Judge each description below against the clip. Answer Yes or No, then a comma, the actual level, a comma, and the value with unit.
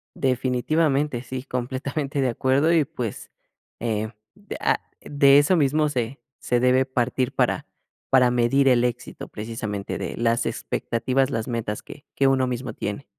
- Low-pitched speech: Yes, low, 130 Hz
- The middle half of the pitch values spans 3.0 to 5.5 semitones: No, narrow, 2.5 semitones